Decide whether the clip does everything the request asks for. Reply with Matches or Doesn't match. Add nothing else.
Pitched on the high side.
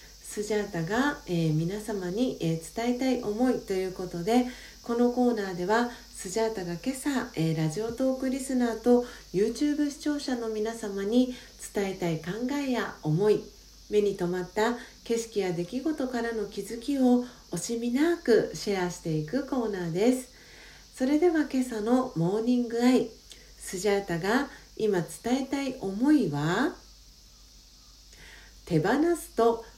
Matches